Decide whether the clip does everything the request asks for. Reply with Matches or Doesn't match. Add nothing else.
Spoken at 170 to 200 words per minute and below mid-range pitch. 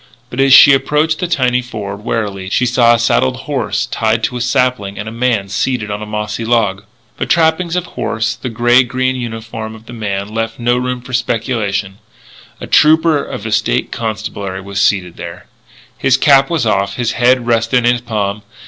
Matches